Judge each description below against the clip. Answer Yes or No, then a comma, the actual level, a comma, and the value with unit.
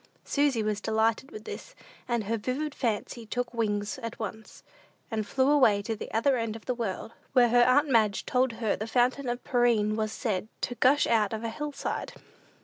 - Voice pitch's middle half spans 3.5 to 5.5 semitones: No, average, 2.7 semitones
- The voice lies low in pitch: No, high, 230 Hz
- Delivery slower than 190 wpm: No, average, 200 wpm